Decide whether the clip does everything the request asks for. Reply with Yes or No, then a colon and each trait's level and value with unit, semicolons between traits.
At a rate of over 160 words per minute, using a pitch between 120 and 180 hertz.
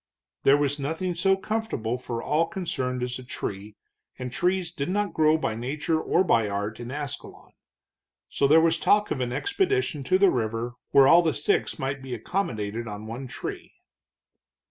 Yes: average, 175 wpm; medium, 140 Hz